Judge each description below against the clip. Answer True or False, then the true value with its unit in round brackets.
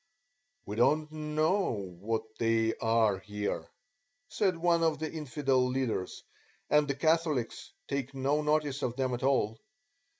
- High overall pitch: False (135 Hz)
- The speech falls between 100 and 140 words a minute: True (135 wpm)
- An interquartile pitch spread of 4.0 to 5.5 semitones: True (5.1 semitones)